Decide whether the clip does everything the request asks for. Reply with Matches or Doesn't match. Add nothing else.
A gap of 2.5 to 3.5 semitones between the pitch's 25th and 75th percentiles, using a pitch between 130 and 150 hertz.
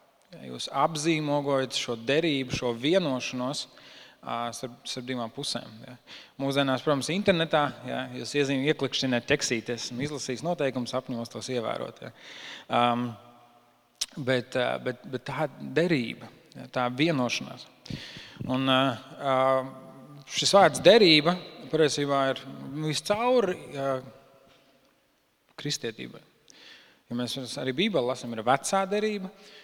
Matches